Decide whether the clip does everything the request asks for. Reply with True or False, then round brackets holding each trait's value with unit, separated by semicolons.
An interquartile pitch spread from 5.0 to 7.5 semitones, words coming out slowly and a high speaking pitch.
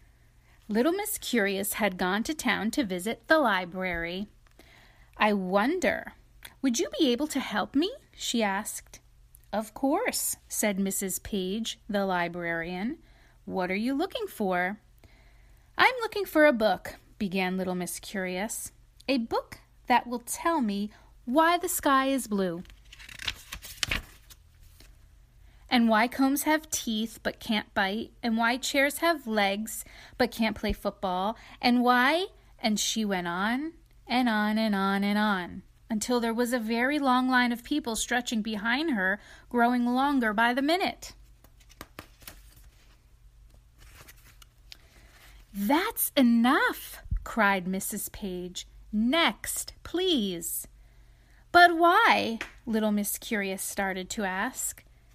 True (5.3 semitones; 125 wpm; 230 Hz)